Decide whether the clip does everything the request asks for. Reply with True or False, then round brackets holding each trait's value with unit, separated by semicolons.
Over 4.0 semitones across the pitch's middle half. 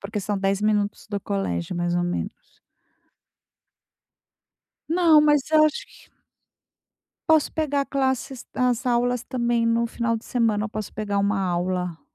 True (4.7 semitones)